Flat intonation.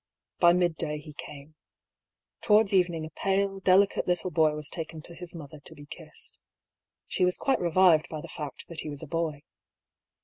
No: average, 3.1 semitones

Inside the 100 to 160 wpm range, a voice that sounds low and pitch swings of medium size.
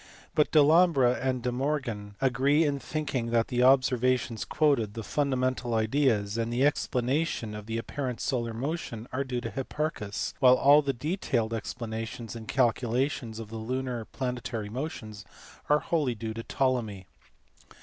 Yes: average, 150 wpm; low, 125 Hz; average, 3.4 semitones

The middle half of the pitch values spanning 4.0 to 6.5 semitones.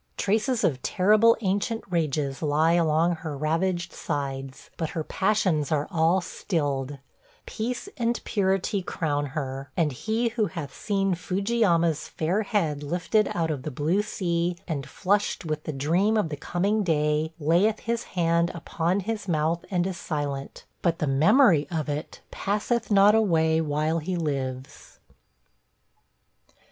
Yes: average, 4.8 semitones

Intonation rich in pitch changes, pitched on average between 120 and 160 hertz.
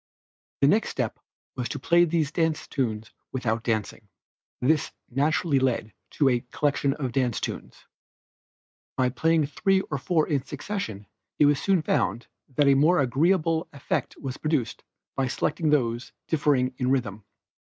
No: average, 4.0 semitones; medium, 140 Hz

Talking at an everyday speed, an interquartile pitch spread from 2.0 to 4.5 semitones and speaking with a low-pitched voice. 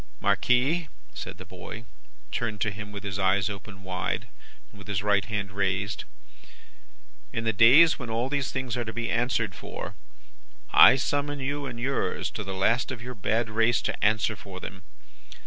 Yes: average, 175 wpm; average, 3.7 semitones; low, 110 Hz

